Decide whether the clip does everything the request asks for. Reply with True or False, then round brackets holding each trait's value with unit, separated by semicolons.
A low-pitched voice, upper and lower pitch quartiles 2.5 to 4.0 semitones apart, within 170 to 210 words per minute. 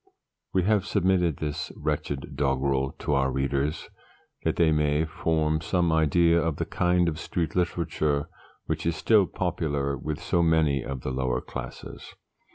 False (80 Hz; 3.4 semitones; 155 wpm)